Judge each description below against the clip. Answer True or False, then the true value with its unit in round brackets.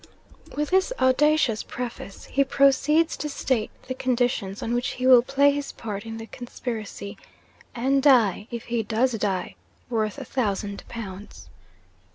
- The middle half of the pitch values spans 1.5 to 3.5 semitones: False (4.0 semitones)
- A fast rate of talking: False (150 wpm)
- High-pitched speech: True (245 Hz)